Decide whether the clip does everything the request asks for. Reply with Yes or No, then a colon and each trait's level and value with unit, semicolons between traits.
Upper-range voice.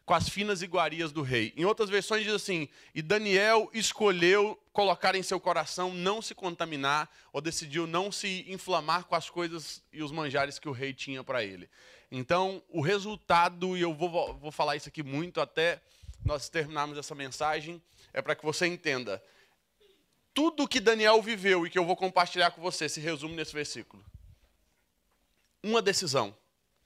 No: medium, 170 Hz